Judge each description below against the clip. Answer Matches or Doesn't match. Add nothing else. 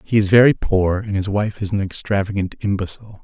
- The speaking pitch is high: Doesn't match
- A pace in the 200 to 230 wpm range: Matches